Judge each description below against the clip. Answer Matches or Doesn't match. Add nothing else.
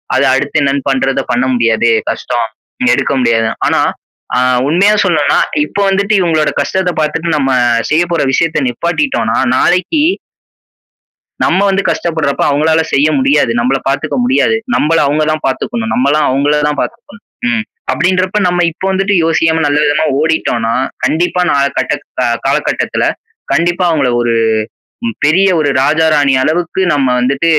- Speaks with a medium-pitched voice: Matches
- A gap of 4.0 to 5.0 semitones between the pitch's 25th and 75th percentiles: Matches